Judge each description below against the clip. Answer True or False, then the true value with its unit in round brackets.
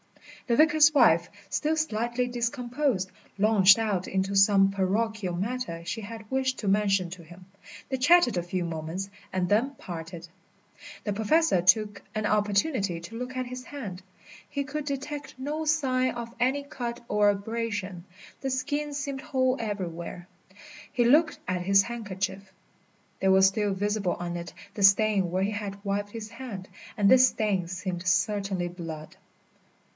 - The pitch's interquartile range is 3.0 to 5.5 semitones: True (5.1 semitones)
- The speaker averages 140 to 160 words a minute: True (155 wpm)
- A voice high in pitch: True (210 Hz)